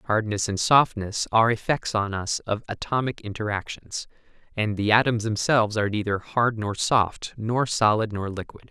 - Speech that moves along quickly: No, average, 160 wpm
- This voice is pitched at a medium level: No, low, 110 Hz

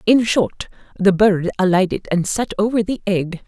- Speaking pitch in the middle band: No, high, 195 Hz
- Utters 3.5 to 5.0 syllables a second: Yes, 4.5 syllables/s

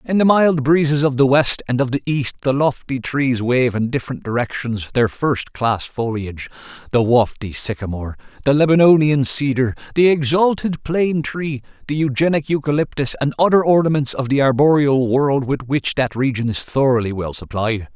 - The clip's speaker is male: Yes, male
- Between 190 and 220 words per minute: No, average, 160 wpm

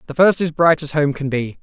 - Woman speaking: No, male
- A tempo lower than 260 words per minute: No, fast, 295 wpm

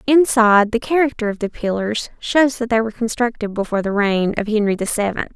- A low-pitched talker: No, high, 225 Hz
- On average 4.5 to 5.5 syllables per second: No, 5.9 syllables/s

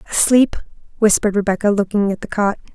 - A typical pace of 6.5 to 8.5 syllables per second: Yes, 6.6 syllables/s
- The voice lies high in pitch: Yes, high, 205 Hz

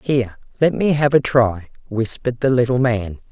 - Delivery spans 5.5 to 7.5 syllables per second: No, 5.2 syllables/s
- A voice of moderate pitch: No, low, 125 Hz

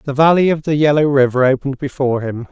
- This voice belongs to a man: Yes, male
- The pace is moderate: No, fast, 215 wpm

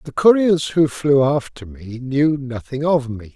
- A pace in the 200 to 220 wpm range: No, average, 180 wpm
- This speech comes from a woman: No, male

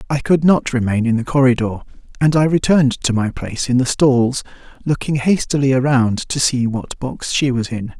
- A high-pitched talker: No, low, 130 Hz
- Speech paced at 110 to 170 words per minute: No, average, 195 wpm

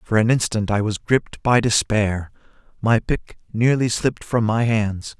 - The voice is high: No, low, 110 Hz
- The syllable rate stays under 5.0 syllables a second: Yes, 4.5 syllables/s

